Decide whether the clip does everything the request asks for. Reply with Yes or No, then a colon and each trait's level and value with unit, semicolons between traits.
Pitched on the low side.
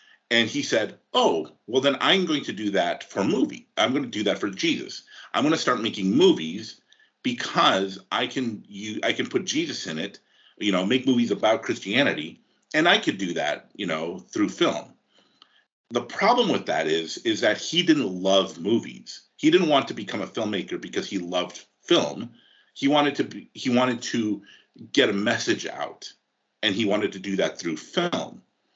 Yes: low, 130 Hz